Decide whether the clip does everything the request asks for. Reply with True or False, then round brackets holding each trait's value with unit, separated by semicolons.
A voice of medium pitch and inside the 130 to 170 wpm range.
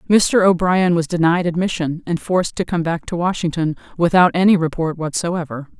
True (170 Hz; 165 wpm)